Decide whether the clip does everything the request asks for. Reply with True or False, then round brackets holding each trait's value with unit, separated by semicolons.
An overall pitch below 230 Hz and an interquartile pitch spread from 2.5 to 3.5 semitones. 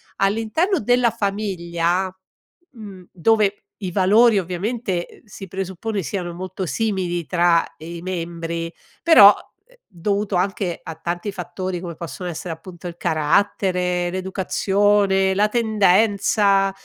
True (190 Hz; 2.8 semitones)